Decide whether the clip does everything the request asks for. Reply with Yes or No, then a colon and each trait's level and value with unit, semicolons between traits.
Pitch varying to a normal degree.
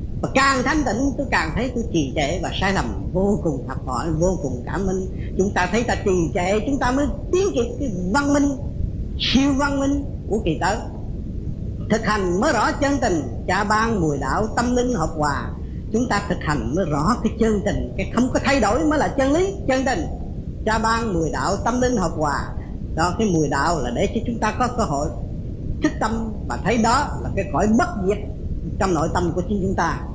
No: wide, 7.5 semitones